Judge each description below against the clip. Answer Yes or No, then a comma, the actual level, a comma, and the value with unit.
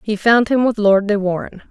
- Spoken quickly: Yes, fast, 245 wpm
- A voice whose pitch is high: Yes, high, 210 Hz